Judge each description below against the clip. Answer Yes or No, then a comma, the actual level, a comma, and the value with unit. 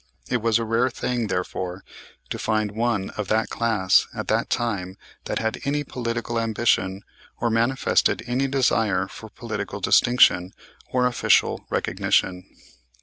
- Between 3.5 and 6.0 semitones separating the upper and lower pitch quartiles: No, average, 3.0 semitones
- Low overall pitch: Yes, low, 115 Hz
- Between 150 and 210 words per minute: No, average, 140 wpm